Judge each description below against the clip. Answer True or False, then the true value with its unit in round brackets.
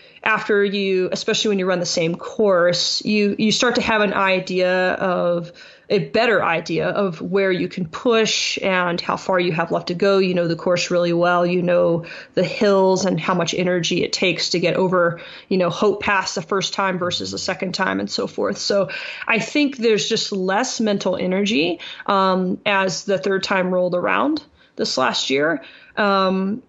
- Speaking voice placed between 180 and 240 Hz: True (190 Hz)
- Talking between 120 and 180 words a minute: False (190 wpm)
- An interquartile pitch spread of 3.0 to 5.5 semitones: False (2.4 semitones)